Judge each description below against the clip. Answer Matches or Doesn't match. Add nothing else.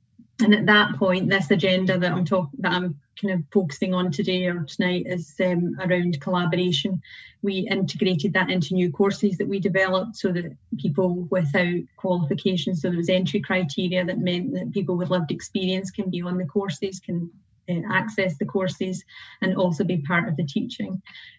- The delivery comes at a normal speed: Matches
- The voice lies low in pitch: Doesn't match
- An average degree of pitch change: Doesn't match